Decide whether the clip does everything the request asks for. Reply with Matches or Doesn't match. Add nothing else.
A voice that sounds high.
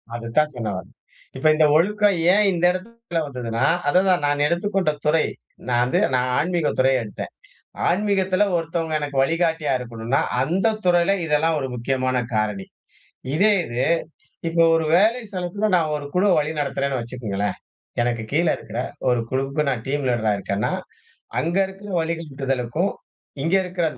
Doesn't match